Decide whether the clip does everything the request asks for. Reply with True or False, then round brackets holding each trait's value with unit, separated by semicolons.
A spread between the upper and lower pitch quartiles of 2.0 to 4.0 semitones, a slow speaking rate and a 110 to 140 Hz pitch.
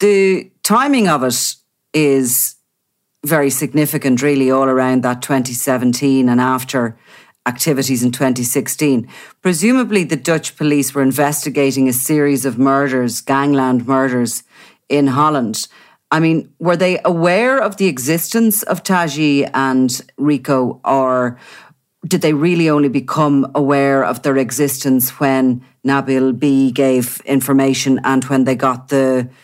True (2.8 semitones; 130 wpm; 135 Hz)